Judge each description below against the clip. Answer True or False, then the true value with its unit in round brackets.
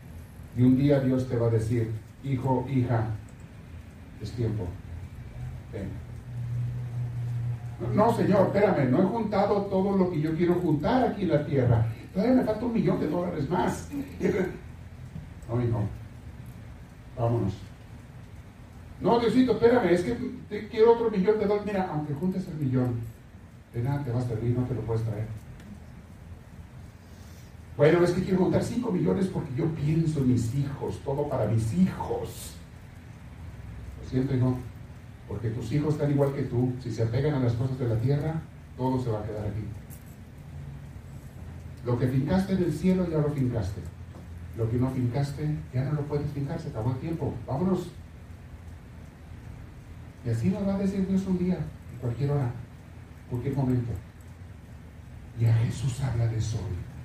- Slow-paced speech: False (160 wpm)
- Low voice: True (125 Hz)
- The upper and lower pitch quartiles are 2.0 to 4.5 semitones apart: False (5.2 semitones)